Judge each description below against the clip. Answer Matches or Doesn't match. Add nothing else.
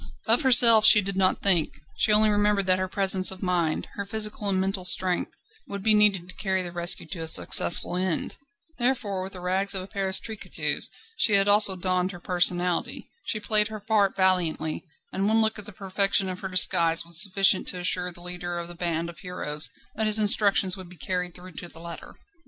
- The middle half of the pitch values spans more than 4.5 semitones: Doesn't match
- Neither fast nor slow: Doesn't match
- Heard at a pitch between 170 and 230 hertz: Matches